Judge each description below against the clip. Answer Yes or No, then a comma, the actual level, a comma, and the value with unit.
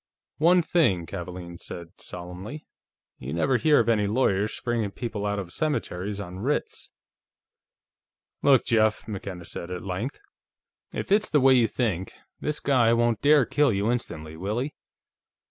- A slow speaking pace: No, average, 150 wpm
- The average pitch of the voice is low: Yes, low, 110 Hz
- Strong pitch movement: Yes, wide, 6.3 semitones